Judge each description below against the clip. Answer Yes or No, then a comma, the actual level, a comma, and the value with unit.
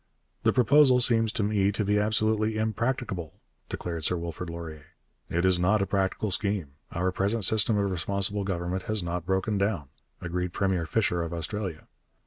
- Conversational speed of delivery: Yes, average, 165 wpm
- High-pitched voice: No, very low, 95 Hz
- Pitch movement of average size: Yes, average, 3.6 semitones